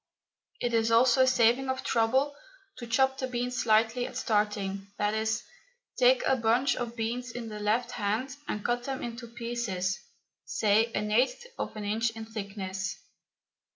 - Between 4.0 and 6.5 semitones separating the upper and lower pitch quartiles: No, average, 2.7 semitones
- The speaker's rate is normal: Yes, average, 160 wpm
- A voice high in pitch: Yes, high, 230 Hz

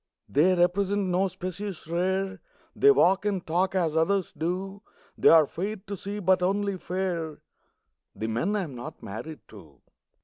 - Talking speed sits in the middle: Yes, average, 150 wpm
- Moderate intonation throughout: Yes, average, 3.1 semitones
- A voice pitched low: No, medium, 185 Hz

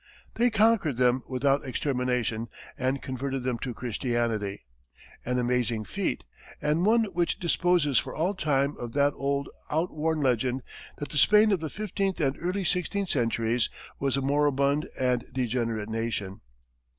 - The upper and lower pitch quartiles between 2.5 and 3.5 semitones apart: No, average, 4.7 semitones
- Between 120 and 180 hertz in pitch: Yes, low, 135 Hz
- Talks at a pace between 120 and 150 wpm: Yes, average, 145 wpm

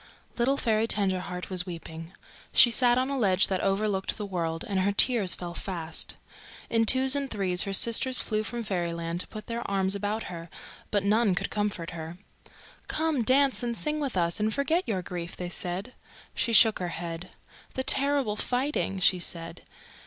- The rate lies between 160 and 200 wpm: Yes, average, 180 wpm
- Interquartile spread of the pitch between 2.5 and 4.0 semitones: No, average, 4.9 semitones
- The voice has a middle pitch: No, high, 200 Hz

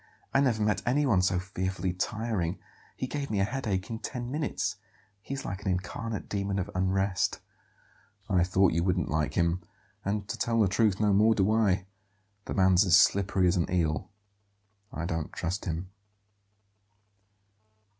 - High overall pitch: No, very low, 95 Hz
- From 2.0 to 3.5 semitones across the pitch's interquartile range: Yes, average, 3.1 semitones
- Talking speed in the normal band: Yes, average, 165 wpm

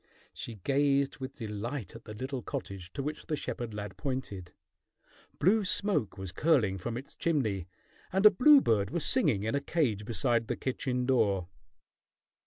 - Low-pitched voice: Yes, low, 125 Hz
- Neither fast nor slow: Yes, average, 160 wpm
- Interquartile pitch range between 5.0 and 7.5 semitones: Yes, wide, 5.6 semitones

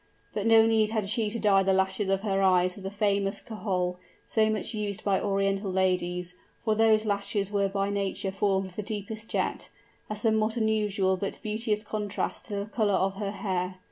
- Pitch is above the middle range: Yes, high, 200 Hz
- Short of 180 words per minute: No, average, 195 wpm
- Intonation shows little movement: Yes, narrow, 1.9 semitones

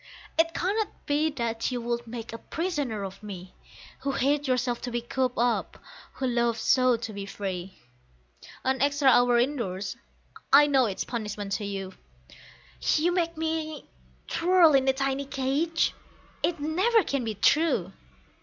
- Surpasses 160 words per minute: No, average, 150 wpm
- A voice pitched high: Yes, very high, 260 Hz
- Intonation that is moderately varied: Yes, average, 4.7 semitones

